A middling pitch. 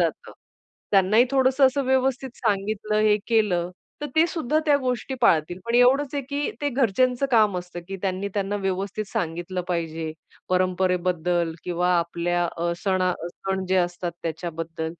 No: high, 195 Hz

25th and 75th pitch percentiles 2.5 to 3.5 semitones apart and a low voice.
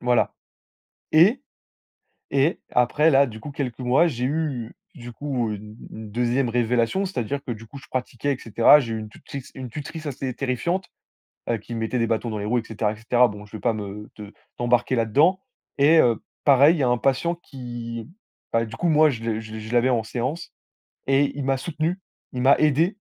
No: average, 3.9 semitones; low, 125 Hz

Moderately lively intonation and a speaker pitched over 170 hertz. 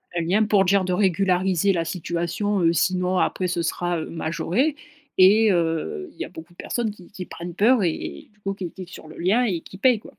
Yes: average, 3.0 semitones; medium, 185 Hz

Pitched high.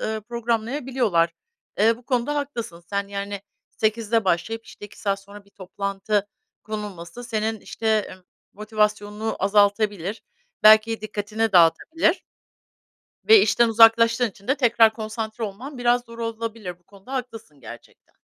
Yes: high, 220 Hz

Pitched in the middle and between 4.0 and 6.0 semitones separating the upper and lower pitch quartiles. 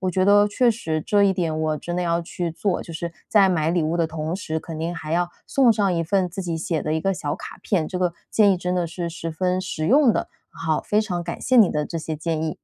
No: medium, 175 Hz; average, 3.2 semitones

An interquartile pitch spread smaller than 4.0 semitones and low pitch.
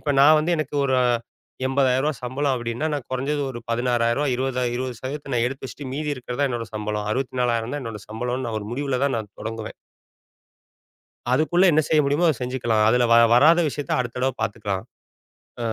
Yes: average, 3.3 semitones; low, 130 Hz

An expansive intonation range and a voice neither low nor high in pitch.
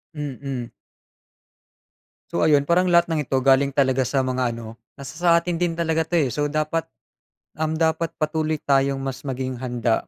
No: average, 3.6 semitones; medium, 145 Hz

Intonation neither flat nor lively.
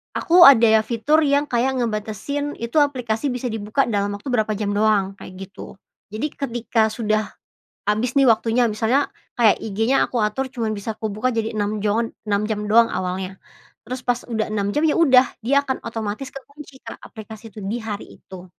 Yes: average, 3.2 semitones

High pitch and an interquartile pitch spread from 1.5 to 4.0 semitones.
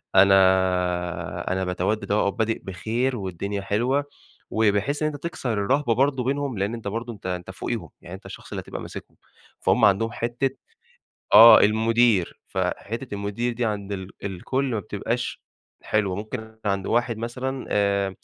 No: low, 105 Hz; average, 3.5 semitones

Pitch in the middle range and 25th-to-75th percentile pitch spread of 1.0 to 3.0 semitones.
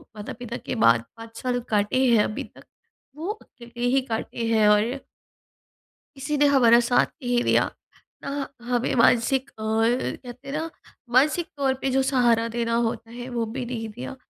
No: high, 245 Hz; average, 2.7 semitones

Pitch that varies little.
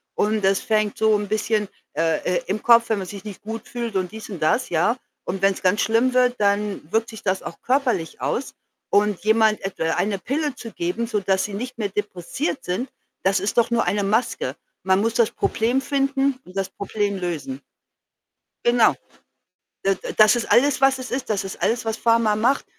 No: average, 3.4 semitones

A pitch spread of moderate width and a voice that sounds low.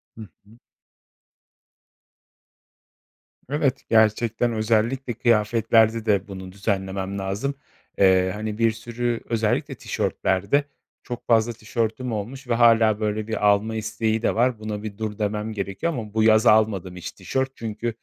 No: narrow, 2.0 semitones; low, 110 Hz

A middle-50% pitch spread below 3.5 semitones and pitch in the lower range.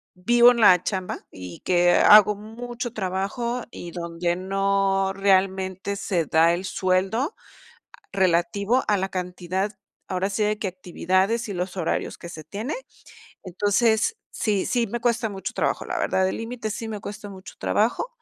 No: average, 3.0 semitones; high, 195 Hz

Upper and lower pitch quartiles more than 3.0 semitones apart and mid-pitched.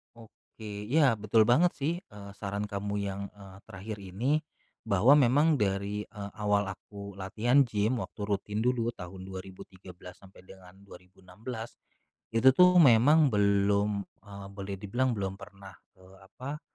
No: average, 3.4 semitones; low, 105 Hz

